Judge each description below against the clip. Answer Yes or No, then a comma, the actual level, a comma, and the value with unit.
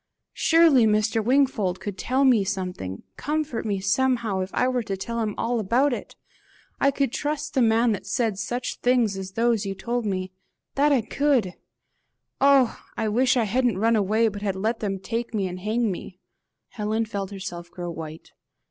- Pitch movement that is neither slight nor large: Yes, average, 4.2 semitones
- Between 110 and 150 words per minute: No, average, 185 wpm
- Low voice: No, high, 220 Hz